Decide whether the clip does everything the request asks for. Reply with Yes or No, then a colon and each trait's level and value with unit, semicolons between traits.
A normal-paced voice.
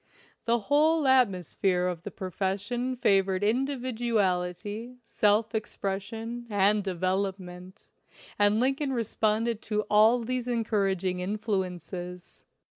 No: slow, 105 wpm